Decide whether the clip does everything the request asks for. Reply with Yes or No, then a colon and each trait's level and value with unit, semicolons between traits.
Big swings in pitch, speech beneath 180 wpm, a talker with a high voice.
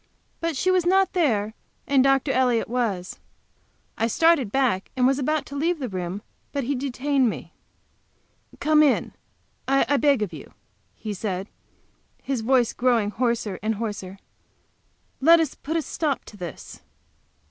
No: average, 4.9 semitones; average, 155 wpm; very high, 255 Hz